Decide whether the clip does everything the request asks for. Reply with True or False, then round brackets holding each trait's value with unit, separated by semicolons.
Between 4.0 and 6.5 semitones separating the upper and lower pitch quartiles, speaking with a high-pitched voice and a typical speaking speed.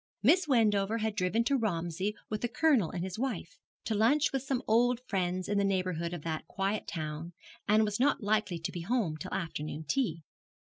True (5.1 semitones; 205 Hz; 195 wpm)